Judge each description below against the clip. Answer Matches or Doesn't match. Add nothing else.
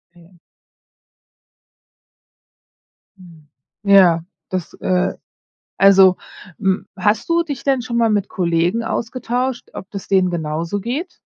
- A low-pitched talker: Doesn't match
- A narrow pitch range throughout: Doesn't match